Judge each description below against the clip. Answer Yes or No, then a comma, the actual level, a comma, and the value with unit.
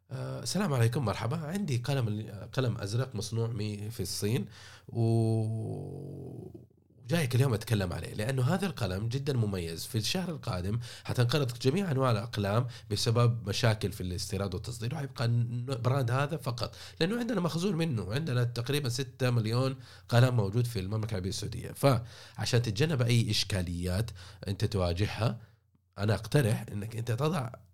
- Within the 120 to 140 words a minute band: Yes, average, 130 wpm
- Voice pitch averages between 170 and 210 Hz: No, low, 120 Hz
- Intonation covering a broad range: No, average, 3.9 semitones